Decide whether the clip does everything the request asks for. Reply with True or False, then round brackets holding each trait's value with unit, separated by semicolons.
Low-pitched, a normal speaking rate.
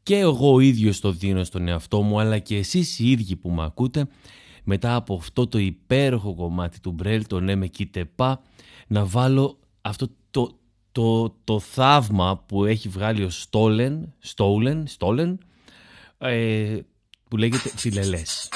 True (110 Hz; 150 wpm)